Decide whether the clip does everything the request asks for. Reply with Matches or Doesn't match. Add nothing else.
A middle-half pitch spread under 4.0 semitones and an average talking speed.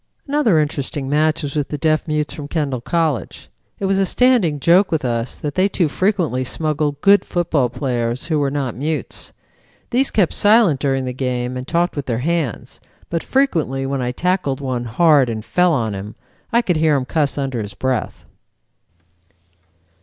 Doesn't match